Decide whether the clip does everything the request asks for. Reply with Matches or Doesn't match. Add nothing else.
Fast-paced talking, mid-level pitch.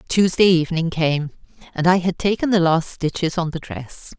Doesn't match